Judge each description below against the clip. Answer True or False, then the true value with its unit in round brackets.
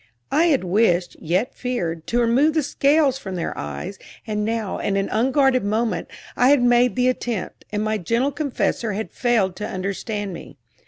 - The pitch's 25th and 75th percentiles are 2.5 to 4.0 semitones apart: False (4.5 semitones)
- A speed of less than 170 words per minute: False (175 wpm)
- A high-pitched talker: True (230 Hz)